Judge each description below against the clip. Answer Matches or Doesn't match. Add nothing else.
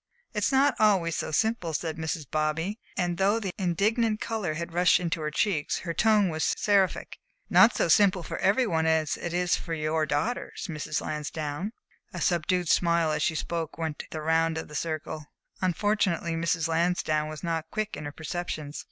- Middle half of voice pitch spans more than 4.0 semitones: Doesn't match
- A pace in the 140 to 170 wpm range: Doesn't match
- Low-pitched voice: Doesn't match